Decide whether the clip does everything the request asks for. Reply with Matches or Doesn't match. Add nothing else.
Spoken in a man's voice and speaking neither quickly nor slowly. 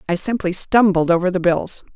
Doesn't match